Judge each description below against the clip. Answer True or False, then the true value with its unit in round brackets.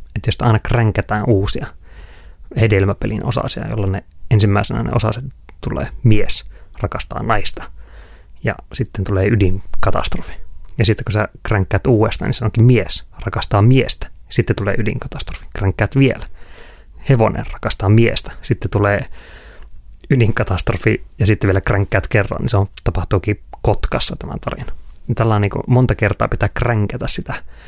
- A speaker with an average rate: True (135 wpm)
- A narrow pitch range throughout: False (3.4 semitones)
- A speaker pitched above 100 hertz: True (110 Hz)